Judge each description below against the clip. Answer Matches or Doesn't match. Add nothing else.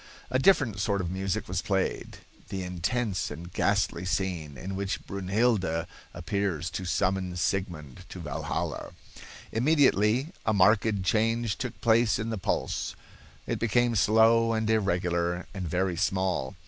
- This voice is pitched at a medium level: Doesn't match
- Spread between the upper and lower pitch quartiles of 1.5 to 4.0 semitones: Matches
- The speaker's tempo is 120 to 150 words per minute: Matches